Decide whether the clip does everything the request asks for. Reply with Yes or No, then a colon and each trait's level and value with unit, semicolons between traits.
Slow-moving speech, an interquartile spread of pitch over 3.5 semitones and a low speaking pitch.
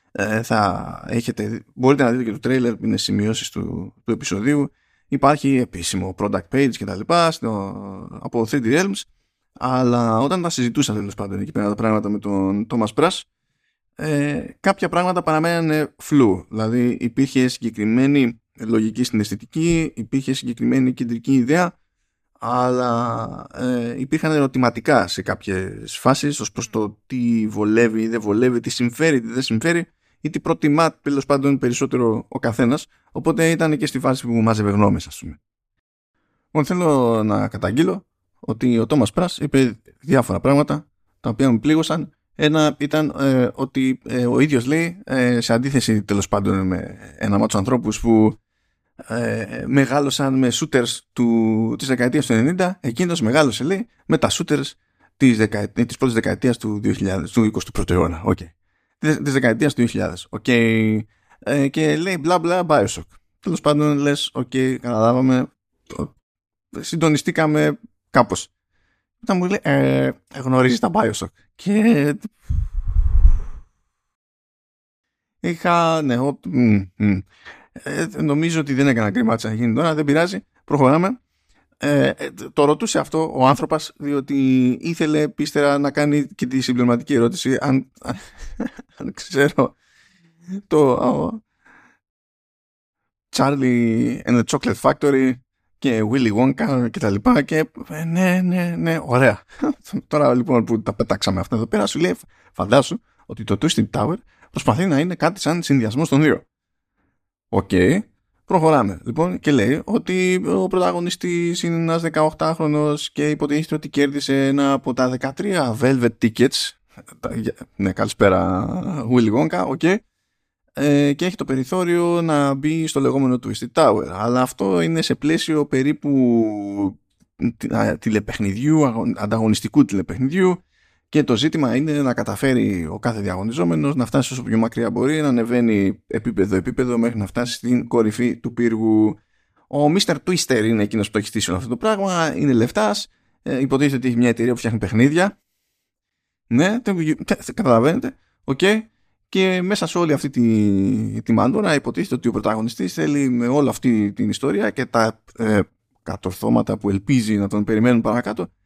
No: average, 145 wpm; average, 5.1 semitones; low, 130 Hz